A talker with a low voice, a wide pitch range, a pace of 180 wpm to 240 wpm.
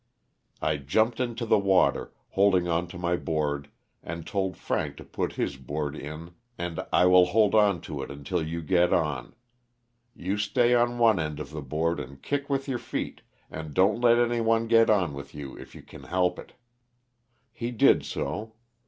Yes: very low, 90 Hz; wide, 6.5 semitones; average, 190 wpm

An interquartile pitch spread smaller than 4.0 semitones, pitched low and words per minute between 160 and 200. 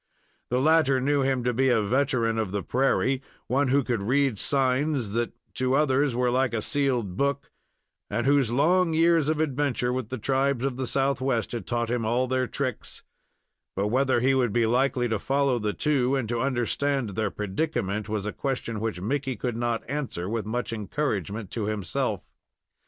Yes: average, 3.3 semitones; low, 125 Hz; average, 185 wpm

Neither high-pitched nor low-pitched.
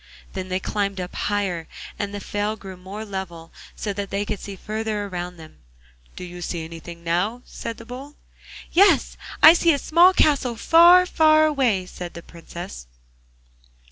No: high, 200 Hz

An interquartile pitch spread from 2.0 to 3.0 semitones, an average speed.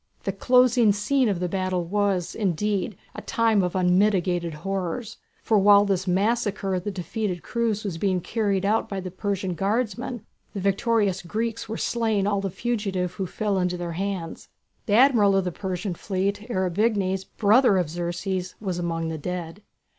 Yes: average, 2.7 semitones; average, 170 wpm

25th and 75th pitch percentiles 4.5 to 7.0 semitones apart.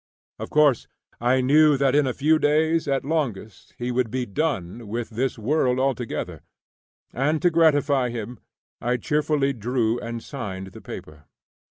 No: average, 4.1 semitones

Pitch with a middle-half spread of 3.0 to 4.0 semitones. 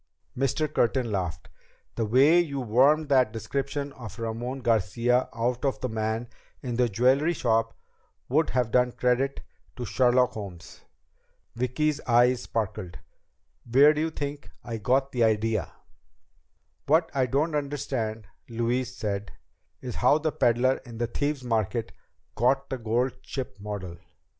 Yes: average, 3.3 semitones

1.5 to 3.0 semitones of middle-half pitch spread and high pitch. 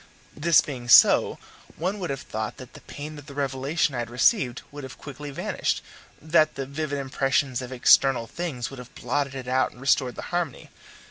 No: average, 2.7 semitones; low, 135 Hz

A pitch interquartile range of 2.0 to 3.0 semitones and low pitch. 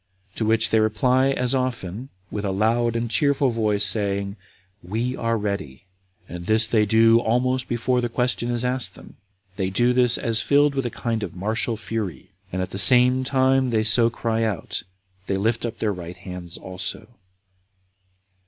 No: average, 3.4 semitones; low, 115 Hz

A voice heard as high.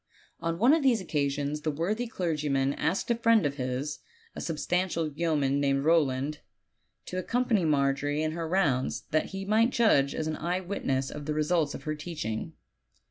No: medium, 155 Hz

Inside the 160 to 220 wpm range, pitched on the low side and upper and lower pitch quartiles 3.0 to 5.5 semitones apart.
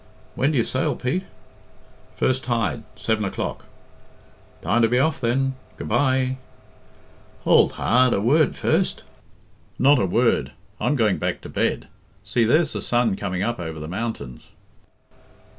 No: average, 145 wpm; low, 120 Hz; average, 3.8 semitones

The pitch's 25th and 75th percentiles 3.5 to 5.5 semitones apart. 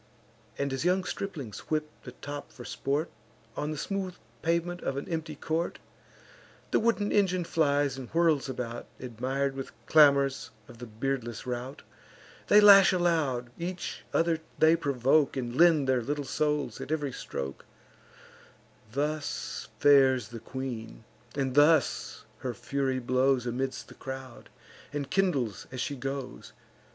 Yes: average, 3.9 semitones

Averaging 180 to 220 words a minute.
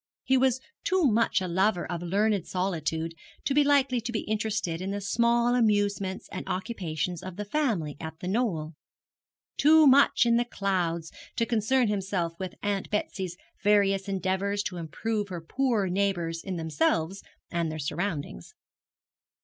No: average, 155 wpm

